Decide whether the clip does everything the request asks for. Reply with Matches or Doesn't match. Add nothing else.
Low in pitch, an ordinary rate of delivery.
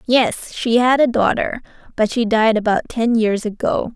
Doesn't match